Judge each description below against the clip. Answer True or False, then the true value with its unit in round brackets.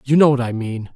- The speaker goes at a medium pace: False (315 wpm)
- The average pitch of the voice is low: True (125 Hz)